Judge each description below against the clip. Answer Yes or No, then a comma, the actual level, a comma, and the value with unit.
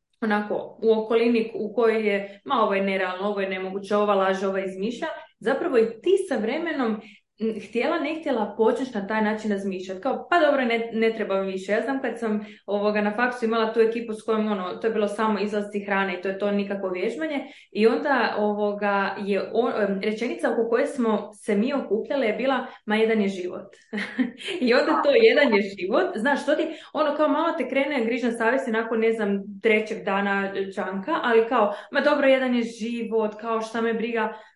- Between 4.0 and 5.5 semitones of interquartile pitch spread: No, average, 3.3 semitones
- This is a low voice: No, high, 220 Hz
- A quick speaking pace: Yes, fast, 195 wpm